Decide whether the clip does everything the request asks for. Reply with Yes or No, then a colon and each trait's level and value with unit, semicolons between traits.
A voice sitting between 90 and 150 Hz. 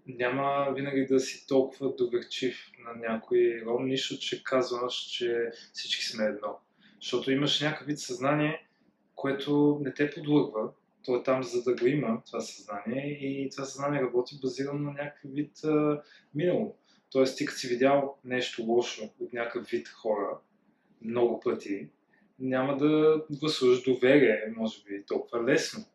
Yes: low, 135 Hz